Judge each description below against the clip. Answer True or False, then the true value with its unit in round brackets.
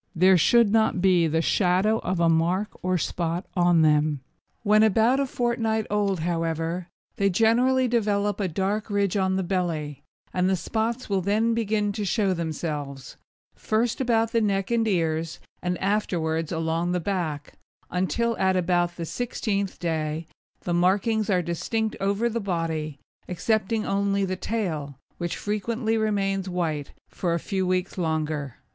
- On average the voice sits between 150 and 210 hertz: True (190 Hz)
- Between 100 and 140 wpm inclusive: False (155 wpm)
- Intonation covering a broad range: False (4.3 semitones)